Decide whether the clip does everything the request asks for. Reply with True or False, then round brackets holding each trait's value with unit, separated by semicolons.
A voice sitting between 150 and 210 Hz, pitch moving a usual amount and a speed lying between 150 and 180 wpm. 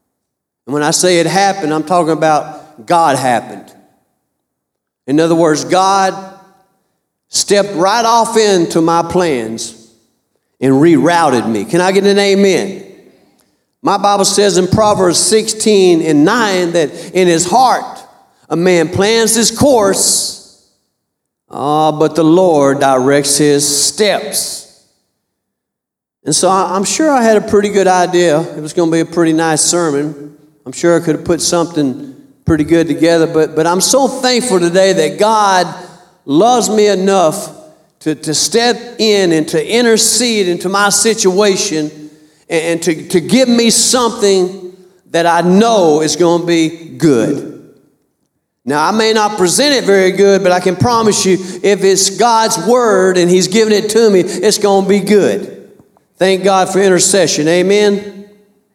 True (185 Hz; 4.0 semitones; 155 wpm)